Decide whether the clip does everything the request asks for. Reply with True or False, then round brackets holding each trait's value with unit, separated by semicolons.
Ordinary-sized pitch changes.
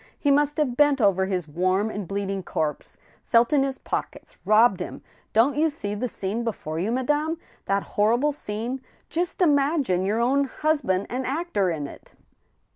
False (6.5 semitones)